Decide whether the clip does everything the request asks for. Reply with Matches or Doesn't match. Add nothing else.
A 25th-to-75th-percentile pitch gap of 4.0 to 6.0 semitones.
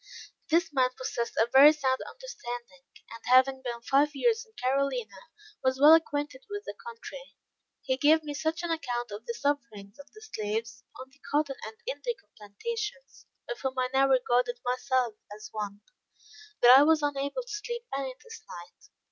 Matches